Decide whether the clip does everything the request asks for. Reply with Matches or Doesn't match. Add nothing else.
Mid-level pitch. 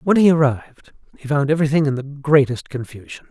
Matches